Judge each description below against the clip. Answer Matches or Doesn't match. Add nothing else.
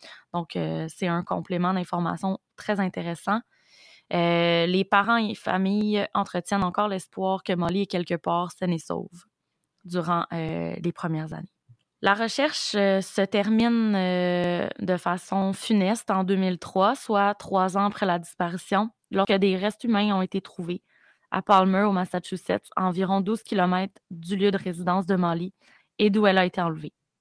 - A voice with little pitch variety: Matches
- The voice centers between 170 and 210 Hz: Matches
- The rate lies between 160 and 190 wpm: Matches